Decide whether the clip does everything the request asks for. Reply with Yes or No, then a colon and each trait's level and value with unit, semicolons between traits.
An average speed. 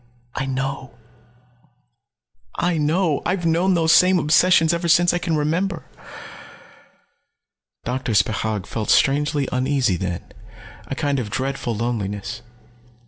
No: slow, 115 wpm